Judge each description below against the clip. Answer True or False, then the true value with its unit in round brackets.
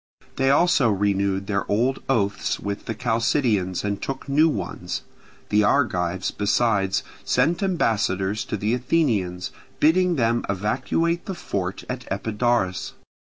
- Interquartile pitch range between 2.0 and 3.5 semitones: False (5.1 semitones)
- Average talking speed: False (125 wpm)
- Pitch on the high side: False (110 Hz)